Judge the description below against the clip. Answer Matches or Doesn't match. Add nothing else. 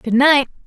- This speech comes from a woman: Matches